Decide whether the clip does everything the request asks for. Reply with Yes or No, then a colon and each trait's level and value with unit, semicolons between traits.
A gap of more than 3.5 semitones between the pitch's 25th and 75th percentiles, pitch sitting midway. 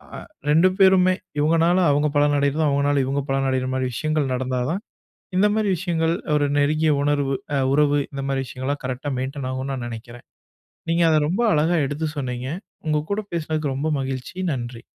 No: average, 3.1 semitones; medium, 145 Hz